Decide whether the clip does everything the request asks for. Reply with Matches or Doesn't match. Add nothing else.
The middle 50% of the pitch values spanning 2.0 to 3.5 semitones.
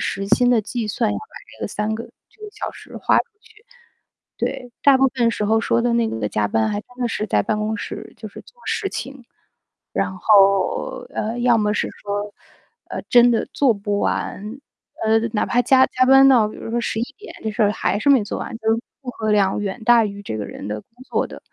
Matches